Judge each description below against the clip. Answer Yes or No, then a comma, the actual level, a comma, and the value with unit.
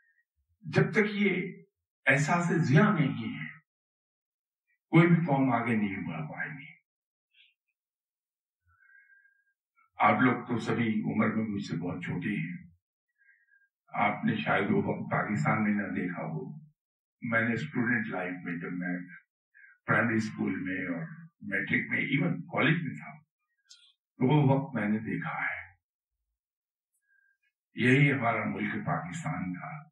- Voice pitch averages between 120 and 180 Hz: Yes, low, 135 Hz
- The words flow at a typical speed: No, slow, 130 wpm